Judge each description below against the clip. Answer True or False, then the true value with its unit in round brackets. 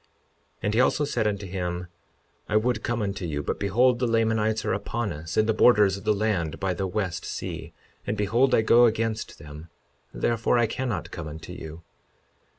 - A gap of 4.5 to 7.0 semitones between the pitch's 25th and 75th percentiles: False (4.0 semitones)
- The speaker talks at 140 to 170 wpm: False (195 wpm)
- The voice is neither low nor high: False (105 Hz)